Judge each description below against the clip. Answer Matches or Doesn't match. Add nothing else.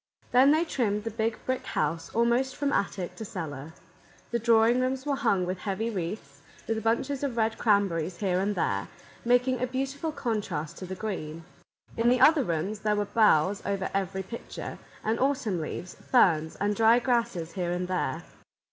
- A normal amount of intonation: Matches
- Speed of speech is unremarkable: Matches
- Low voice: Doesn't match